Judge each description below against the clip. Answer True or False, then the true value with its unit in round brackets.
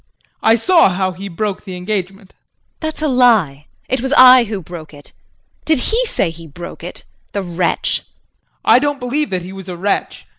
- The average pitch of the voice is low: False (200 Hz)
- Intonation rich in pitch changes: True (6.1 semitones)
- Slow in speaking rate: False (195 wpm)